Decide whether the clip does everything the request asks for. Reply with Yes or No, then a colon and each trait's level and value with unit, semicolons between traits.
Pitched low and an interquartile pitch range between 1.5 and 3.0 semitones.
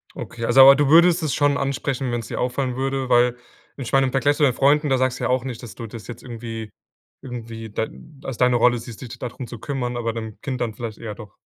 Yes: low, 125 Hz; average, 2.7 semitones